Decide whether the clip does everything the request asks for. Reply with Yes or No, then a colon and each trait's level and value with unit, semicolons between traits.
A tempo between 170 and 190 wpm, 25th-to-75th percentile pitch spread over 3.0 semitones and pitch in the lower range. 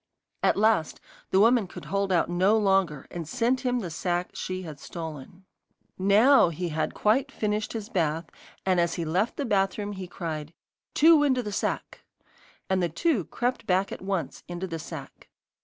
No: average, 175 wpm; average, 4.2 semitones; high, 190 Hz